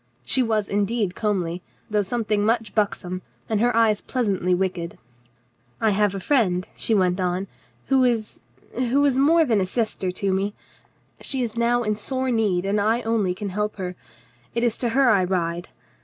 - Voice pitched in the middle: No, high, 210 Hz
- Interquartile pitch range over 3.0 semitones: Yes, average, 3.9 semitones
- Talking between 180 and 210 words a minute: Yes, average, 185 wpm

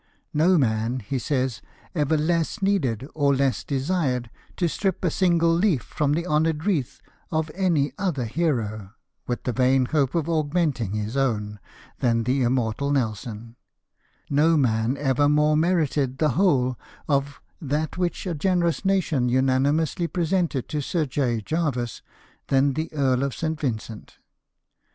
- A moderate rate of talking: Yes, average, 145 wpm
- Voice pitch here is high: No, medium, 140 Hz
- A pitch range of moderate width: Yes, average, 4.5 semitones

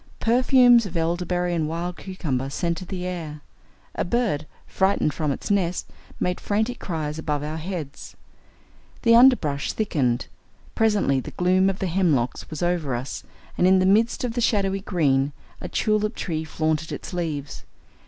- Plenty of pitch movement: No, average, 4.4 semitones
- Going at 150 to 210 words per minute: Yes, average, 155 wpm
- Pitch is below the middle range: No, medium, 175 Hz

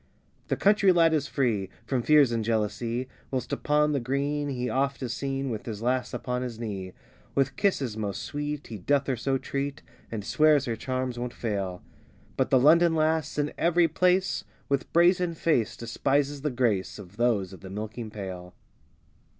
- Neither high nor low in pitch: No, low, 130 Hz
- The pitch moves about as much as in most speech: Yes, average, 4.7 semitones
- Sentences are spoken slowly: No, average, 175 wpm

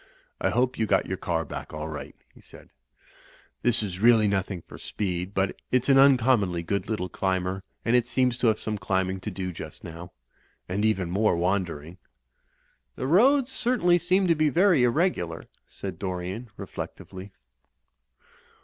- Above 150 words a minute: Yes, average, 165 wpm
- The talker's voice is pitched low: Yes, low, 100 Hz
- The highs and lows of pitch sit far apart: Yes, wide, 5.8 semitones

